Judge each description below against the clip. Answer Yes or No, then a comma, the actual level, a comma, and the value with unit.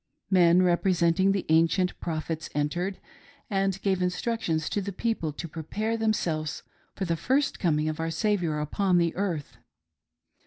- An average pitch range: Yes, average, 3.4 semitones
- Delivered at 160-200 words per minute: No, average, 140 wpm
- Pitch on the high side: No, medium, 180 Hz